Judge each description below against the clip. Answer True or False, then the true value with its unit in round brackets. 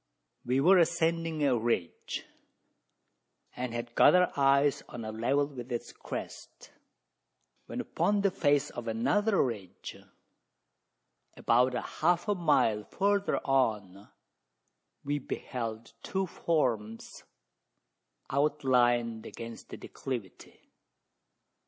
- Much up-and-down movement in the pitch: True (5.7 semitones)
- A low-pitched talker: True (130 Hz)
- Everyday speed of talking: False (100 wpm)